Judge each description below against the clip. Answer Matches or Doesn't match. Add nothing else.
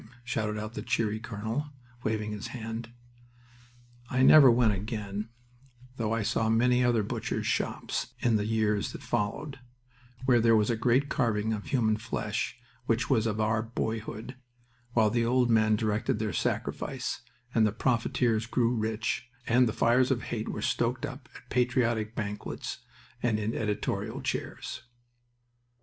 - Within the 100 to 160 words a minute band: Matches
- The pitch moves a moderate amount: Doesn't match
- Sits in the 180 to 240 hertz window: Doesn't match